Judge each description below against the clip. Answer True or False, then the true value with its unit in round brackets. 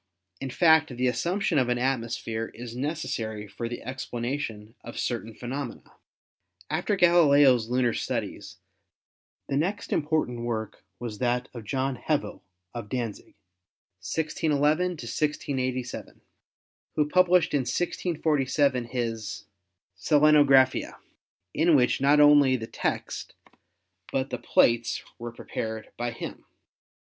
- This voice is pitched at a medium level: False (130 Hz)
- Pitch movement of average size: True (4.0 semitones)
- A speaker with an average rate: False (120 wpm)